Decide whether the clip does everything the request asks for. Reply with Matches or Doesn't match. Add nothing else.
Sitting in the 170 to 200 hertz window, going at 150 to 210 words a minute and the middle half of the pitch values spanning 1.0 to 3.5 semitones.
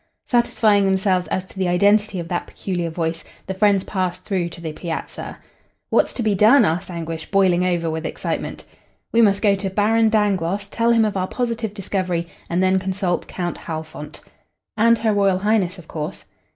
Matches